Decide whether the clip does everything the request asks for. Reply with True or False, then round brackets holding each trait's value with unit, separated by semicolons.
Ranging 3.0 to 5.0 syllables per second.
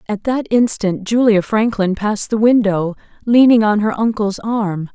True (4.4 syllables/s)